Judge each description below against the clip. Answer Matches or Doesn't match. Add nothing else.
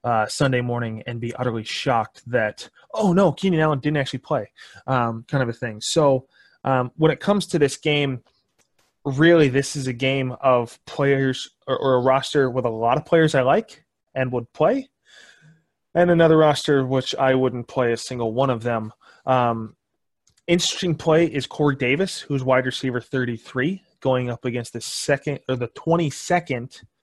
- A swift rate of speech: Doesn't match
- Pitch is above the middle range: Doesn't match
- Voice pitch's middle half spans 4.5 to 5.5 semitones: Doesn't match